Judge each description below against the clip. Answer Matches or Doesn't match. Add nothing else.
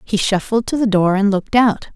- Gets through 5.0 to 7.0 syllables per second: Matches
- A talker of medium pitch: Doesn't match